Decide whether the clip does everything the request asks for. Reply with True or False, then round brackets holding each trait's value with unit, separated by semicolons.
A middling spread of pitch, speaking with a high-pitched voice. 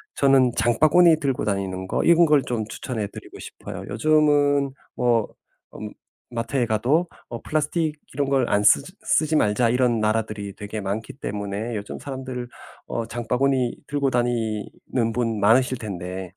False (4.4 semitones; 120 Hz)